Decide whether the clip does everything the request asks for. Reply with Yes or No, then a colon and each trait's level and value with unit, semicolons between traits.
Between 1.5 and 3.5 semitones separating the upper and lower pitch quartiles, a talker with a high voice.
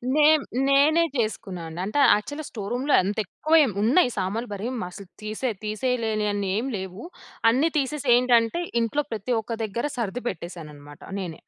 No: average, 5.2 semitones; high, 225 Hz